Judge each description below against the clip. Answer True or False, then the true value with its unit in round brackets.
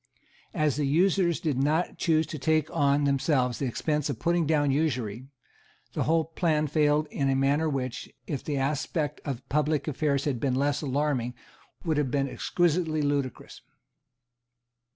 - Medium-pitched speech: True (145 Hz)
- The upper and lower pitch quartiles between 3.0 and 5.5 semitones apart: False (2.4 semitones)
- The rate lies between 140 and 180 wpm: True (155 wpm)